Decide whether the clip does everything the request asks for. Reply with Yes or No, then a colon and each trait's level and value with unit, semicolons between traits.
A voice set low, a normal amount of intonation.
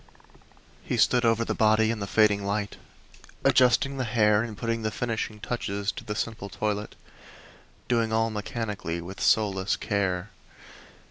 No: low, 110 Hz; narrow, 2.1 semitones